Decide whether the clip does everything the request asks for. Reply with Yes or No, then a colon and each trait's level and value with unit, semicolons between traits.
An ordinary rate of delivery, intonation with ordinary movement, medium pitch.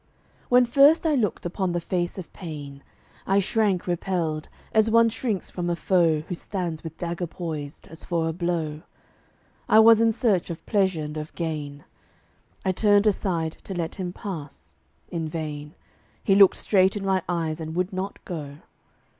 Yes: average, 170 wpm; average, 3.7 semitones; medium, 175 Hz